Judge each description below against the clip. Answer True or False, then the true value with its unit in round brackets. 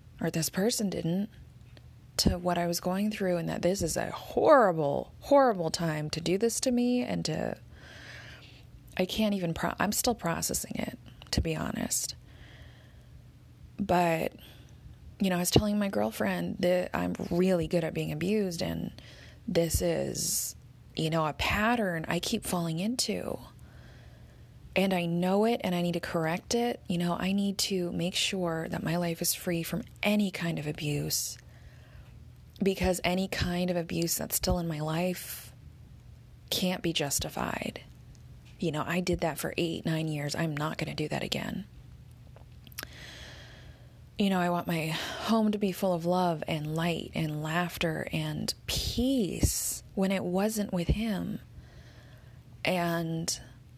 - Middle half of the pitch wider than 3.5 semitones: False (2.8 semitones)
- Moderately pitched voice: True (175 Hz)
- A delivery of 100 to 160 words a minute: True (155 wpm)